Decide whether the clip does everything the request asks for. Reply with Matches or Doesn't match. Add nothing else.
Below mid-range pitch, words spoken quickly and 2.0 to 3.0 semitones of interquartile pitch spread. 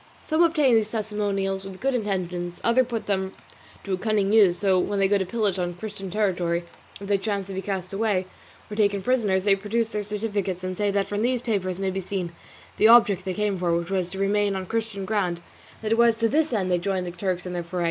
Doesn't match